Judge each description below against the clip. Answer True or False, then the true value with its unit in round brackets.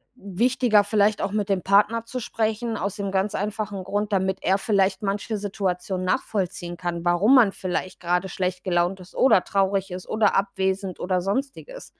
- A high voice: True (195 Hz)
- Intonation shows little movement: True (2.3 semitones)